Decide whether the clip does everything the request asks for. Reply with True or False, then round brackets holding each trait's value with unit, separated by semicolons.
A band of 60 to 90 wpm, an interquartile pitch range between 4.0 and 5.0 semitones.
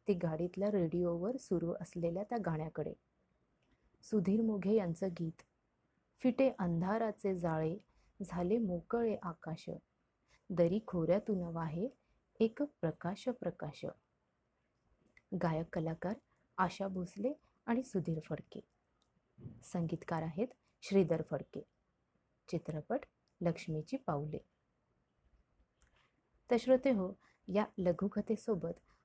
True (80 wpm; 4.4 semitones)